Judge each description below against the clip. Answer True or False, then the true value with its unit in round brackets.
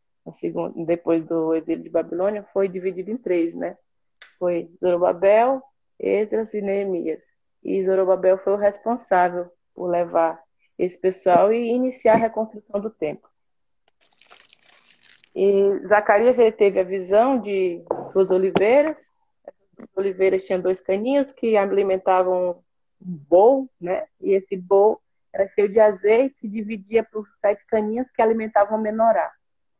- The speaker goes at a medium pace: True (130 wpm)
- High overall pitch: True (200 Hz)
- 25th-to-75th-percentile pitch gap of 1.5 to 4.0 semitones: True (3.1 semitones)